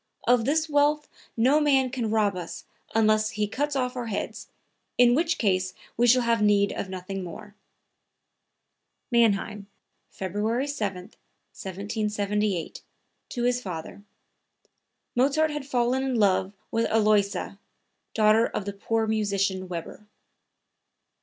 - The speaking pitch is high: Yes, high, 215 Hz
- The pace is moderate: No, slow, 125 wpm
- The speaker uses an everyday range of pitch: Yes, average, 3.8 semitones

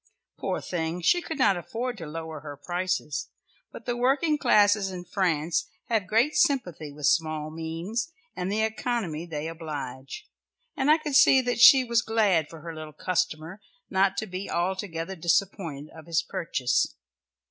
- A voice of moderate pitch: Yes, medium, 180 Hz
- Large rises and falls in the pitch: Yes, wide, 5.8 semitones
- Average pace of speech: Yes, average, 160 wpm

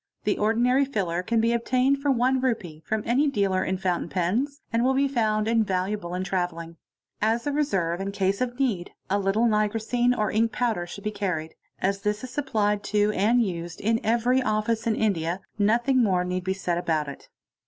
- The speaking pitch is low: No, high, 210 Hz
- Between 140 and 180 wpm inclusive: No, average, 190 wpm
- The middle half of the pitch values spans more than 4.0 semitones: Yes, average, 4.4 semitones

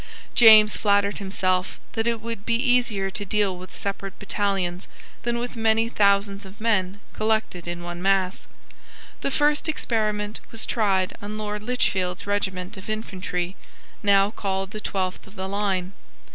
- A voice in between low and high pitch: No, high, 200 Hz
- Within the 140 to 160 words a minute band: Yes, average, 150 wpm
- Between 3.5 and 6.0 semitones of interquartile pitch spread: No, narrow, 2.5 semitones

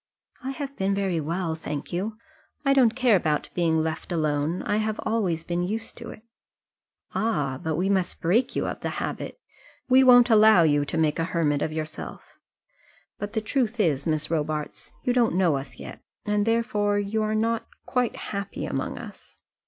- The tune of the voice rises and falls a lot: Yes, wide, 5.7 semitones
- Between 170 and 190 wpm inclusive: Yes, average, 185 wpm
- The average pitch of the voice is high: Yes, high, 195 Hz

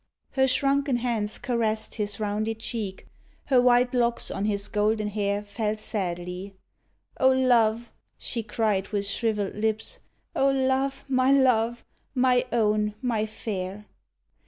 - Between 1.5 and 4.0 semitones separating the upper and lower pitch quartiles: Yes, average, 3.2 semitones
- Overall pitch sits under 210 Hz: No, high, 220 Hz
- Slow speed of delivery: Yes, slow, 130 wpm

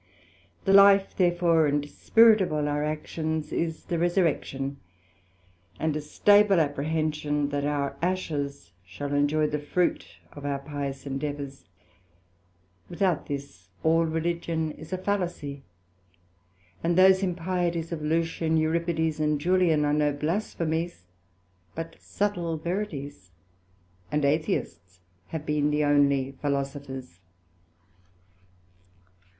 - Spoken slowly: Yes, slow, 110 wpm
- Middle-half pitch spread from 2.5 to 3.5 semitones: Yes, average, 3.0 semitones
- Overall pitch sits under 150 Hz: No, medium, 155 Hz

